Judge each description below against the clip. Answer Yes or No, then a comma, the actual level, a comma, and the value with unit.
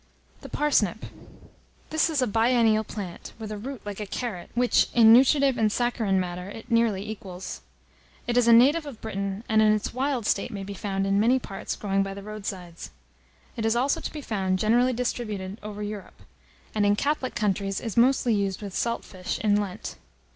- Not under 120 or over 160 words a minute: No, average, 195 wpm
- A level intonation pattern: No, average, 3.5 semitones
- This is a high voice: Yes, high, 215 Hz